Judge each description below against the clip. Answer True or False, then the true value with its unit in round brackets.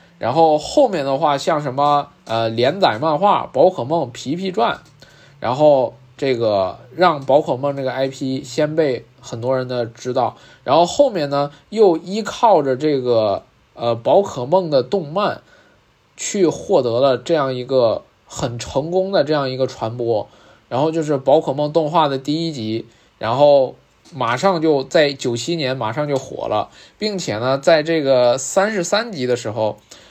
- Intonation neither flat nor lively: True (4.2 semitones)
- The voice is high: False (140 Hz)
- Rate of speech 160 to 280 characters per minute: True (230 characters per minute)